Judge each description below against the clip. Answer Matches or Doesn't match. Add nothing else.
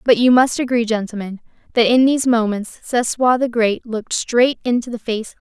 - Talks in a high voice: Matches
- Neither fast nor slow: Doesn't match